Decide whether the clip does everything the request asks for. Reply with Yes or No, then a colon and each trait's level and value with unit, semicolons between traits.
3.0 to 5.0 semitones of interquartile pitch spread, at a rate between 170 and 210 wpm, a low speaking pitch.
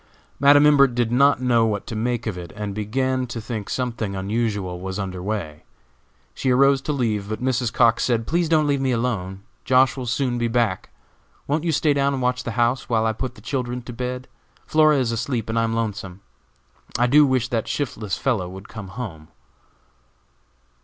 Yes: average, 3.4 semitones; average, 195 wpm; low, 120 Hz